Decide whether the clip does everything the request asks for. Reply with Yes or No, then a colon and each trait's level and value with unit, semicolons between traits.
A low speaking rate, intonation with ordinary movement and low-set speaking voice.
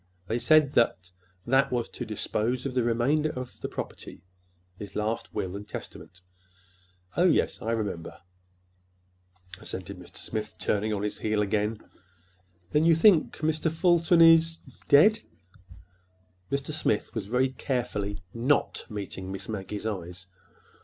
No: slow, 125 wpm; wide, 6.5 semitones; low, 115 Hz